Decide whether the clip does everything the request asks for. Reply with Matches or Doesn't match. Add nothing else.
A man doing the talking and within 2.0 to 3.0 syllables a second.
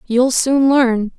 Doesn't match